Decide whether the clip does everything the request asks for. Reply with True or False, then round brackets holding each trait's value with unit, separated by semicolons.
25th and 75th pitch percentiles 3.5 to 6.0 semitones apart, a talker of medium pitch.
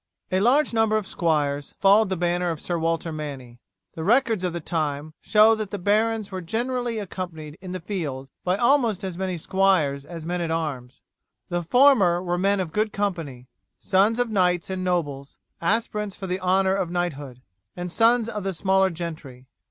True (4.1 semitones; 180 Hz)